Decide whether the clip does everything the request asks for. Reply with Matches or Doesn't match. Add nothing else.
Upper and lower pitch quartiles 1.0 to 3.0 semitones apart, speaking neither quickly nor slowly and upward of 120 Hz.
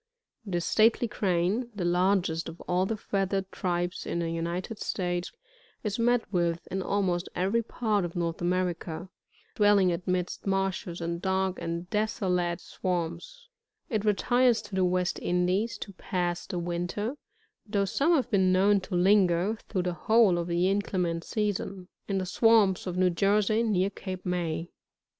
Matches